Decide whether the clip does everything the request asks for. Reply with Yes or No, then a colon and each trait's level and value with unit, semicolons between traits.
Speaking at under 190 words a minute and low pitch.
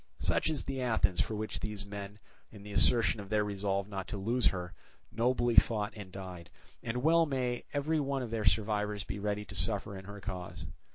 No: fast, 205 wpm; low, 105 Hz